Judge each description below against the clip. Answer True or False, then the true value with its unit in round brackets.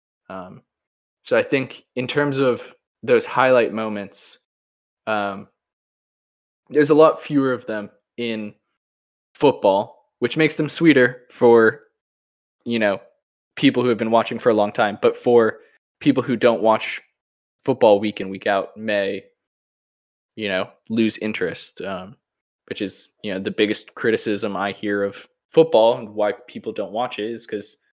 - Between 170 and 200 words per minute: False (150 wpm)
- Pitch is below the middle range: True (110 Hz)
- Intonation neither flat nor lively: True (3.5 semitones)